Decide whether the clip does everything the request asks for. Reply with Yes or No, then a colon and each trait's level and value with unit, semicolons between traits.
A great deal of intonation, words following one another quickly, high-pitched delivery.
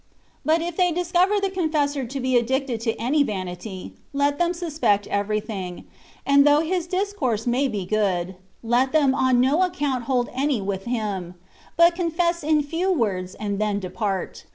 No: wide, 7.4 semitones; average, 165 wpm; very high, 260 Hz